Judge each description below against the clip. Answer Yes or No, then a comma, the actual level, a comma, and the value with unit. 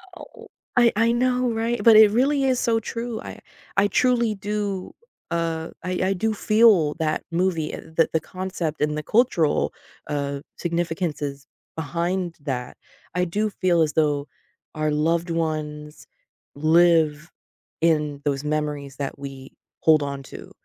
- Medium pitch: Yes, medium, 165 Hz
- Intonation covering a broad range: Yes, wide, 5.9 semitones